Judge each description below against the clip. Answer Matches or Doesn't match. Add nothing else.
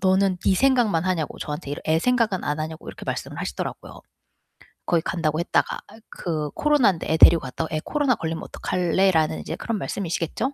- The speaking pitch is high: Doesn't match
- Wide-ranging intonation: Doesn't match